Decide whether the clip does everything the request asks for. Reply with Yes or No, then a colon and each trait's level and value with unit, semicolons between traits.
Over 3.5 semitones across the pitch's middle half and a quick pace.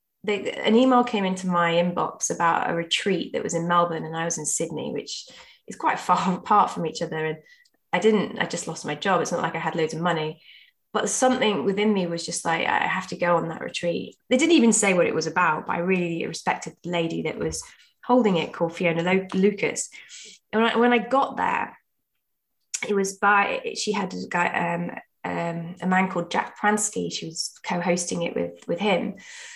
Yes: average, 3.9 semitones; fast, 220 wpm